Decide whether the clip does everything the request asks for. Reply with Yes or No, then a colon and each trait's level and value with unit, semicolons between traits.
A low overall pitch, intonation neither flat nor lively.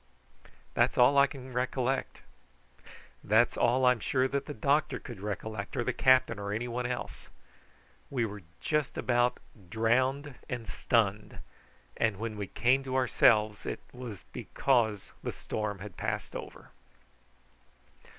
Yes: low, 120 Hz; average, 3.3 semitones